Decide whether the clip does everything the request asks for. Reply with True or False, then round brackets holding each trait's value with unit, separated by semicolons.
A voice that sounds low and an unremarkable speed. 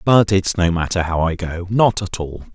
False (90 Hz; 210 wpm)